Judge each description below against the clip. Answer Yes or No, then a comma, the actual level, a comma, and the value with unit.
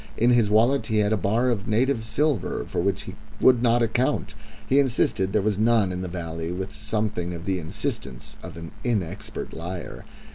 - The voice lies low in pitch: Yes, low, 105 Hz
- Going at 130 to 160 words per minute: No, average, 190 wpm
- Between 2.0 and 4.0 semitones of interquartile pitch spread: No, average, 4.5 semitones